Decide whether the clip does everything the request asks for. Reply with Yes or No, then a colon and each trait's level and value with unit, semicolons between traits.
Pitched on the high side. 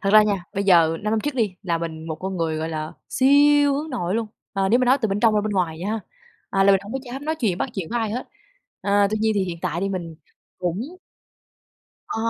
Yes: high, 200 Hz